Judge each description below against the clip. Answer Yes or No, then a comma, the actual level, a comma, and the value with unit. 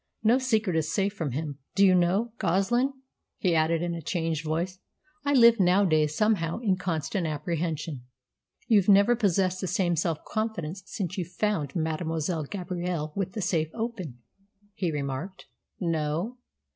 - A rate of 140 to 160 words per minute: Yes, average, 150 wpm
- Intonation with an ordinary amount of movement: Yes, average, 3.9 semitones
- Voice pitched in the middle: Yes, medium, 180 Hz